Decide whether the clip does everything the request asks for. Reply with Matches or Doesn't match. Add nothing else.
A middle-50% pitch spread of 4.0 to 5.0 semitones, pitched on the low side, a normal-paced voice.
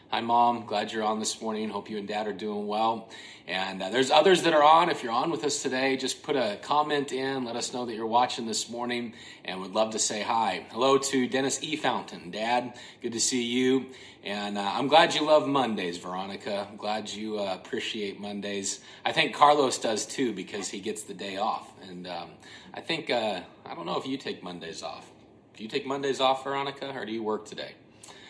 Doesn't match